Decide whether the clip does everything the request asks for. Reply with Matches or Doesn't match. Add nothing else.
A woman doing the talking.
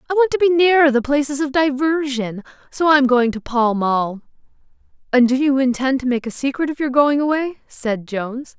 Matches